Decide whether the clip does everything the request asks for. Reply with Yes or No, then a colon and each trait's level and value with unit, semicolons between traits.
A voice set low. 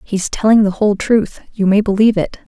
No: high, 205 Hz